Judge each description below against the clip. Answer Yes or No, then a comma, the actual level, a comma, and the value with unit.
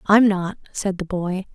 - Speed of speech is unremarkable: Yes, average, 195 wpm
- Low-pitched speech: No, high, 190 Hz